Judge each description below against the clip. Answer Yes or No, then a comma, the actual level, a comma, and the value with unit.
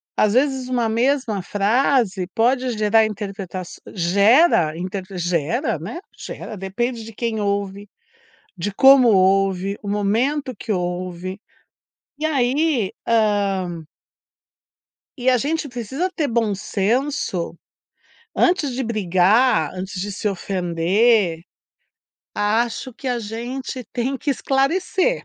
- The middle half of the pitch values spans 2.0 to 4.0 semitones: No, average, 5.0 semitones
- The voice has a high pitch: Yes, high, 215 Hz